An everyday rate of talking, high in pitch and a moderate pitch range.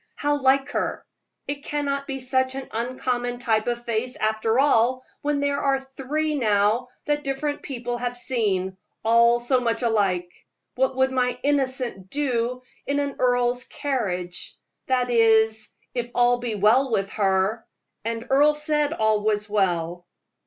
Yes: average, 150 wpm; high, 245 Hz; average, 3.5 semitones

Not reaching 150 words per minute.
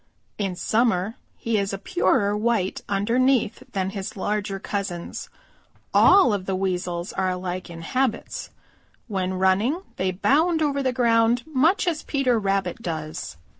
Yes: average, 140 wpm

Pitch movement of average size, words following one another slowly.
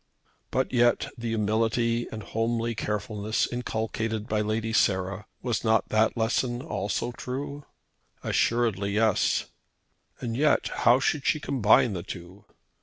No: narrow, 2.2 semitones; slow, 125 wpm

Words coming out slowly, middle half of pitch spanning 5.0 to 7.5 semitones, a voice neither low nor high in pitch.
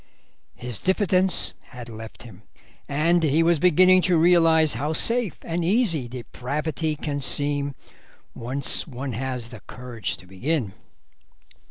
Yes: slow, 130 wpm; wide, 5.4 semitones; medium, 145 Hz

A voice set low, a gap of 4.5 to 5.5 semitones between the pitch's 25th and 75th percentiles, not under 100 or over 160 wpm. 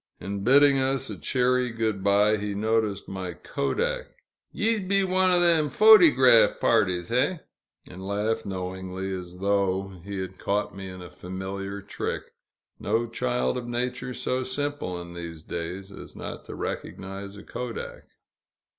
Yes: low, 105 Hz; average, 5.2 semitones; average, 150 wpm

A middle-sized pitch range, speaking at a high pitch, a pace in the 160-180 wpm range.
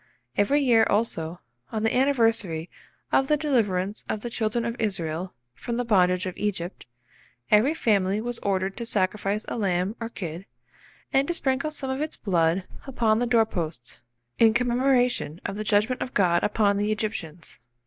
Yes: average, 4.5 semitones; high, 215 Hz; average, 170 wpm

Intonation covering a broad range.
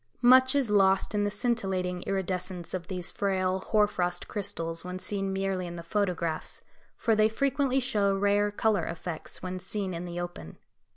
No: average, 2.7 semitones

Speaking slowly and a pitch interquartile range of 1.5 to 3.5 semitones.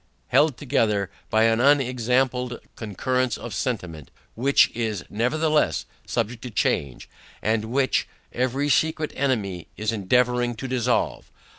Yes: slow, 120 wpm; average, 3.2 semitones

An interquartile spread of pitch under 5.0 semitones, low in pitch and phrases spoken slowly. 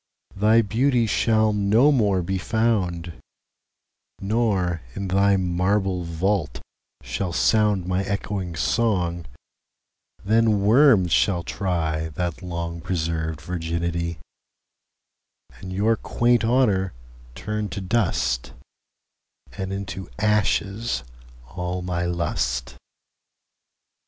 Yes: average, 3.7 semitones; very low, 95 Hz; slow, 80 wpm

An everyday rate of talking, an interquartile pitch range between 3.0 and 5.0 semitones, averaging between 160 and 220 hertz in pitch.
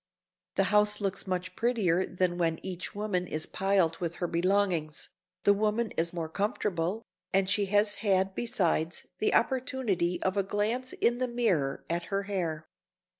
Yes: average, 160 wpm; average, 3.3 semitones; high, 190 Hz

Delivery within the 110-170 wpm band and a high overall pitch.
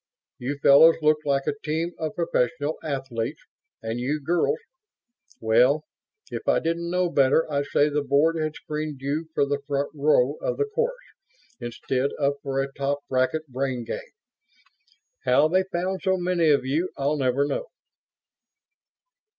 No: average, 155 wpm; medium, 145 Hz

